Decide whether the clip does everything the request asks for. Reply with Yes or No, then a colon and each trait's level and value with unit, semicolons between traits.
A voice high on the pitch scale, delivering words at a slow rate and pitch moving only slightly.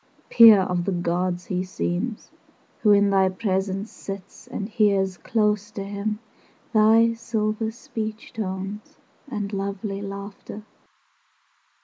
Yes: high, 200 Hz; slow, 120 wpm; narrow, 2.0 semitones